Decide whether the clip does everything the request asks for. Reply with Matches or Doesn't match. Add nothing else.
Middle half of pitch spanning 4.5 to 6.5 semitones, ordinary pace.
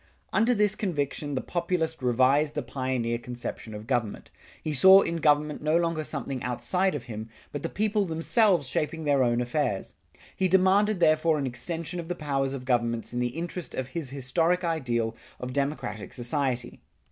Matches